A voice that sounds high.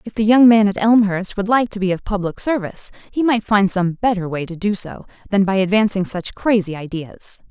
Yes: high, 200 Hz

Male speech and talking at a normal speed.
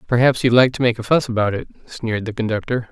No: male; fast, 245 wpm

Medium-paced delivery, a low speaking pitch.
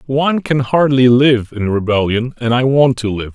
Yes: average, 195 wpm; low, 125 Hz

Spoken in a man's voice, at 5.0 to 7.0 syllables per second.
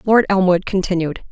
No: female; 5.2 syllables/s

